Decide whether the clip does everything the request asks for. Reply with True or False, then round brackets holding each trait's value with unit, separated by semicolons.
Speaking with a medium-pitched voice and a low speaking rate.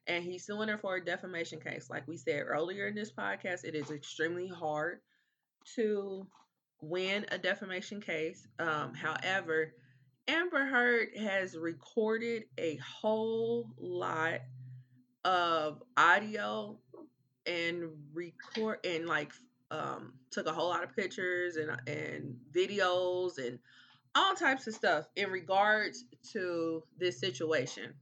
True (180 Hz; 125 wpm)